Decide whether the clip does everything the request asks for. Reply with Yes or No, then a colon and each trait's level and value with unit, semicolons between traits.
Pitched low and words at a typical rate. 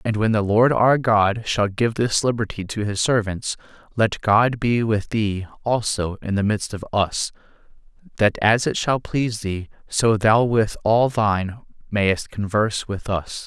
Yes: low, 110 Hz; average, 175 wpm